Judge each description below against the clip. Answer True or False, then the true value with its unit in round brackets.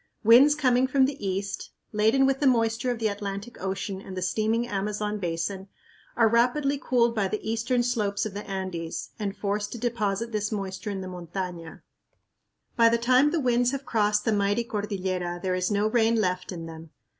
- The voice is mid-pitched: False (210 Hz)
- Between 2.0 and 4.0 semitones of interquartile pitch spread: True (3.6 semitones)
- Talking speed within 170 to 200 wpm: True (190 wpm)